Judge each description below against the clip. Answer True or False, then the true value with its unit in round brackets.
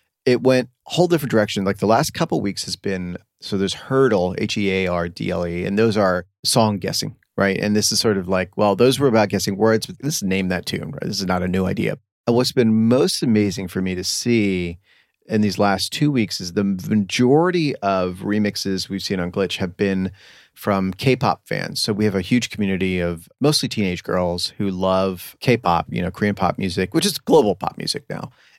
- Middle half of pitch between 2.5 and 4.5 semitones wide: True (3.3 semitones)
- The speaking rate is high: True (230 wpm)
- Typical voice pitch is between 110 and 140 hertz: False (100 Hz)